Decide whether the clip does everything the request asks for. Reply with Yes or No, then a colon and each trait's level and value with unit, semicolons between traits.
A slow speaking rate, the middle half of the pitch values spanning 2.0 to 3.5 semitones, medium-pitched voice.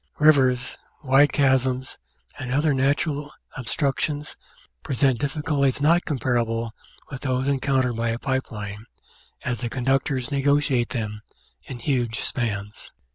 No: slow, 125 wpm; average, 2.8 semitones; low, 130 Hz